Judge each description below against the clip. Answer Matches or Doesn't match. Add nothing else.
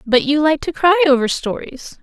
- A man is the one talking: Doesn't match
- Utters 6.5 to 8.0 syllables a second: Doesn't match